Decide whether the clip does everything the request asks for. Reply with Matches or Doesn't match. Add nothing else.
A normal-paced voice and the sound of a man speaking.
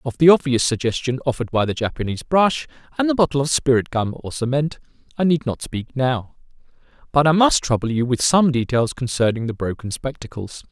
Matches